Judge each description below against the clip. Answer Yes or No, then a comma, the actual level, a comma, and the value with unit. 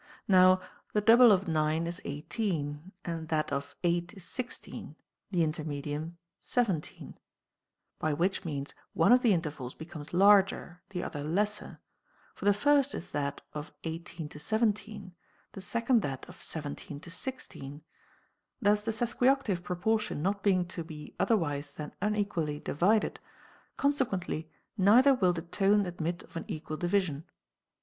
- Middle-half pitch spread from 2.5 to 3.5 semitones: No, average, 5.0 semitones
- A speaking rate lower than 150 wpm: Yes, average, 140 wpm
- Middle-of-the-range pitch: Yes, medium, 175 Hz